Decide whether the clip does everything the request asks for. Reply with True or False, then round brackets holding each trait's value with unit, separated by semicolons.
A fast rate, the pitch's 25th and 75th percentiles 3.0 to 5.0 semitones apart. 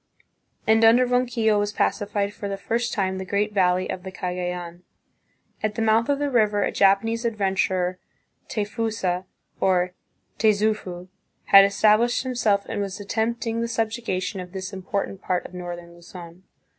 False (155 wpm; 3.3 semitones)